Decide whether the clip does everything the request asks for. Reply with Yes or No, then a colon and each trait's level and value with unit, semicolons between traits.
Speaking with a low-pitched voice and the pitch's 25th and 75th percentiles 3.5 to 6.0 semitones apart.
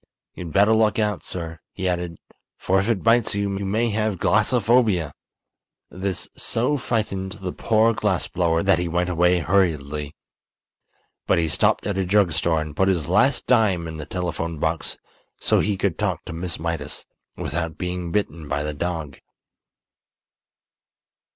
Yes: very low, 90 Hz; average, 3.9 semitones